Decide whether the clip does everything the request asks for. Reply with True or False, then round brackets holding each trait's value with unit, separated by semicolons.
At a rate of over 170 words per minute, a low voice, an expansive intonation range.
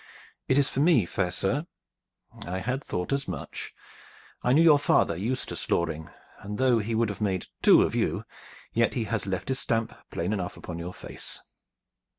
True (180 wpm; 110 Hz; 6.1 semitones)